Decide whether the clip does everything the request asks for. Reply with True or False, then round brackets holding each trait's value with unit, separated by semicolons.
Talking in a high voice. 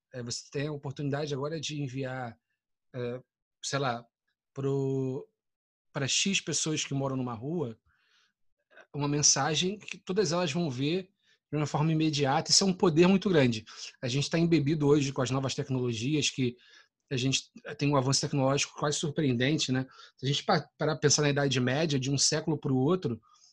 False (140 Hz)